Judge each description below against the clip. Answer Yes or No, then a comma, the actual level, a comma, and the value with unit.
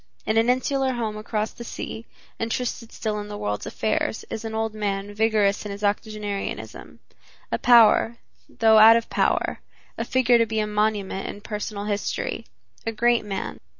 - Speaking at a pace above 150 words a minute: Yes, average, 170 wpm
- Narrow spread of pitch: Yes, narrow, 1.6 semitones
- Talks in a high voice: Yes, high, 215 Hz